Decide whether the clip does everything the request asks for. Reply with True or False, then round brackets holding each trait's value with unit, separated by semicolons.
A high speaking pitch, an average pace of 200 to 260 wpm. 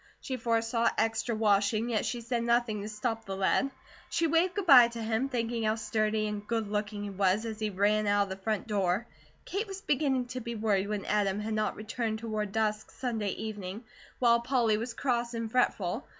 True (220 Hz; 205 wpm)